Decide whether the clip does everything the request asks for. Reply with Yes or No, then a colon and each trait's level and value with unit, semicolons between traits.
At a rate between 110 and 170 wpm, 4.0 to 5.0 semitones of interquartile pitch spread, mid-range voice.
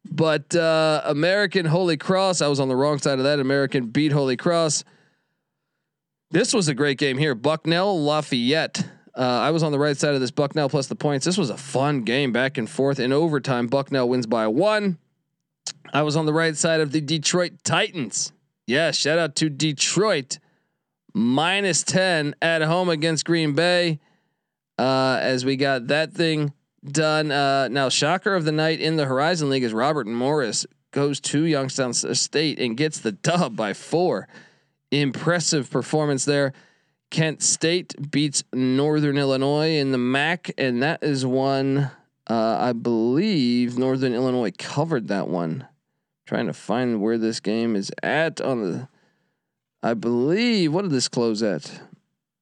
No: average, 165 wpm; average, 3.4 semitones; medium, 145 Hz